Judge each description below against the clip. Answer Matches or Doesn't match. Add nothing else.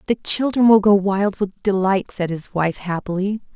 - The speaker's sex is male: Doesn't match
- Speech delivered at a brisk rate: Doesn't match